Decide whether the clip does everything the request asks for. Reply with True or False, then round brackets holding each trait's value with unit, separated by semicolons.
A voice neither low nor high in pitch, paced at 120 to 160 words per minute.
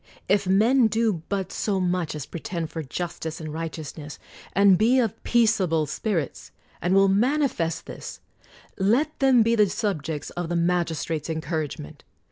True (180 Hz; 150 wpm)